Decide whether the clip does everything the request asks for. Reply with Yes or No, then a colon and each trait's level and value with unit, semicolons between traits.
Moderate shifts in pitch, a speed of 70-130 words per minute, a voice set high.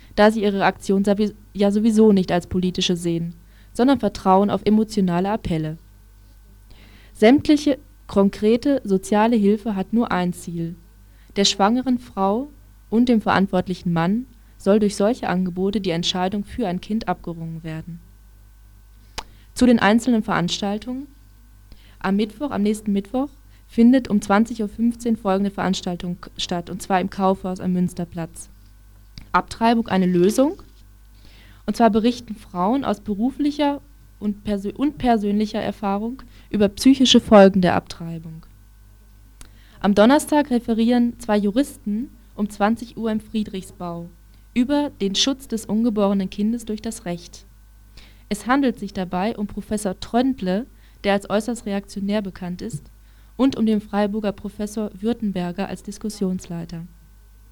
Yes: average, 4.2 semitones; slow, 125 wpm; high, 200 Hz